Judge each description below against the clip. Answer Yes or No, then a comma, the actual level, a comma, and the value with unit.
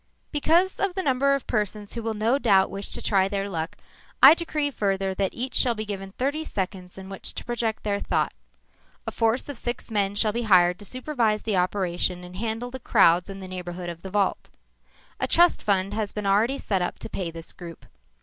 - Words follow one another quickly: Yes, fast, 215 wpm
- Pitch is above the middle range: Yes, high, 205 Hz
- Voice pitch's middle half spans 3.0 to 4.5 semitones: Yes, average, 4.1 semitones